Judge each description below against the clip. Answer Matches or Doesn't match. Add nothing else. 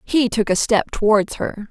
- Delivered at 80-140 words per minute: Doesn't match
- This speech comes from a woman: Matches